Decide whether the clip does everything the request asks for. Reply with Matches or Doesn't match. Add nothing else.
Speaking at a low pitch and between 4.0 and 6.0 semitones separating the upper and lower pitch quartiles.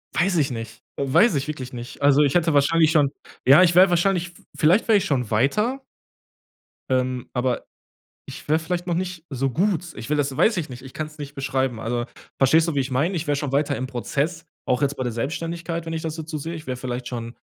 Doesn't match